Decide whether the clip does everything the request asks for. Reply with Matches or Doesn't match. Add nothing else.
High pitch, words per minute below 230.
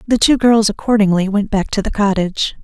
Matches